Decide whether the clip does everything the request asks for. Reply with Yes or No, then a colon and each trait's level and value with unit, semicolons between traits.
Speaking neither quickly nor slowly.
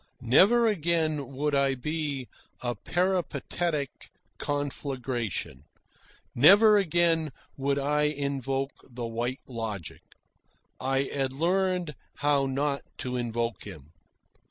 No: slow, 100 wpm